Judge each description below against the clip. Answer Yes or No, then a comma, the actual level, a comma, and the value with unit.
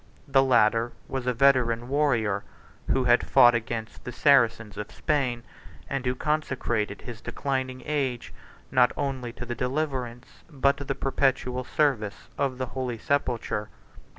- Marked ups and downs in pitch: No, narrow, 2.6 semitones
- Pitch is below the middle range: Yes, low, 125 Hz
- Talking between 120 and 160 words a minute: Yes, average, 145 wpm